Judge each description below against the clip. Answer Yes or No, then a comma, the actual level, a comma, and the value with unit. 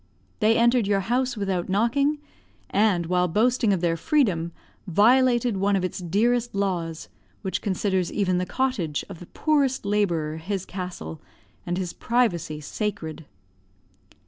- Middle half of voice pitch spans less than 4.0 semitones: No, average, 5.2 semitones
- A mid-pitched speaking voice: No, high, 195 Hz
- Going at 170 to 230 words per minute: No, average, 140 wpm